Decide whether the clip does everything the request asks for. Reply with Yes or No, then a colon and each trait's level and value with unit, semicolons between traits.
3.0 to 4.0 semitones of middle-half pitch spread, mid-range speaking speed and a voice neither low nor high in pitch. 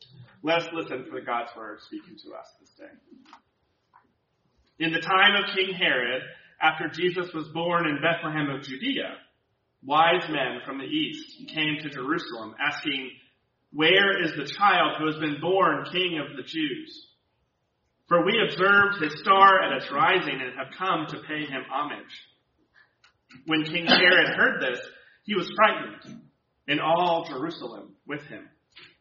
No: average, 4.8 semitones; average, 155 wpm; medium, 165 Hz